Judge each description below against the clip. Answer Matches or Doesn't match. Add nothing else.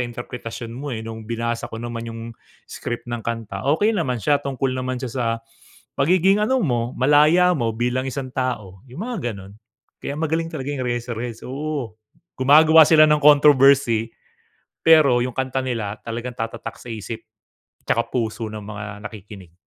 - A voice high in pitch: Doesn't match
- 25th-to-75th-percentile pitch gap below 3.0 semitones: Doesn't match